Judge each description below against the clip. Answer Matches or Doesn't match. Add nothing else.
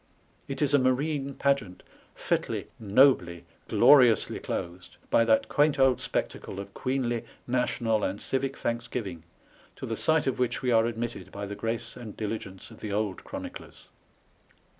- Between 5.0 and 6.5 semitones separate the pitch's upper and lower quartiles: Doesn't match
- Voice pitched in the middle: Doesn't match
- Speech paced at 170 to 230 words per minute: Doesn't match